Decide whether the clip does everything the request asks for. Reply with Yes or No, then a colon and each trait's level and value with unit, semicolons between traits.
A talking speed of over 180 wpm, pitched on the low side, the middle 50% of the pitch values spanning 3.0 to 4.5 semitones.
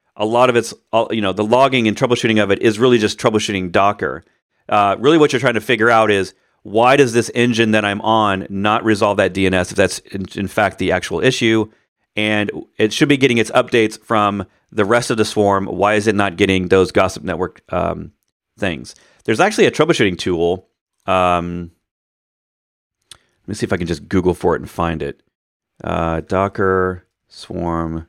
Yes: average, 190 wpm; low, 105 Hz; average, 3.3 semitones